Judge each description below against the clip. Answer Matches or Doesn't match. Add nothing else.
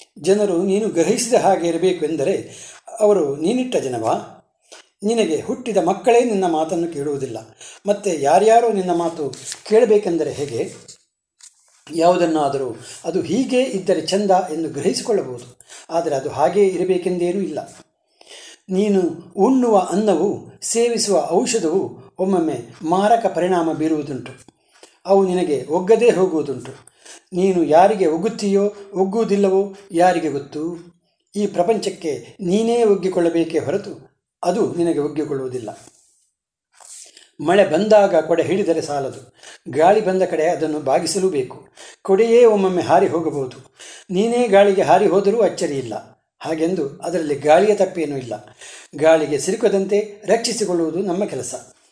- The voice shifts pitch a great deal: Doesn't match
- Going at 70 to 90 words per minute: Doesn't match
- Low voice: Doesn't match